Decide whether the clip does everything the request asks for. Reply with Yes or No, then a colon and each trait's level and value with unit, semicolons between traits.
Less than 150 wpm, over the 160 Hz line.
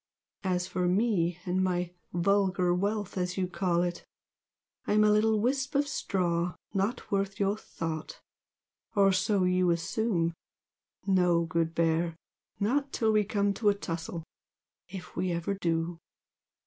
Yes: average, 140 wpm; medium, 185 Hz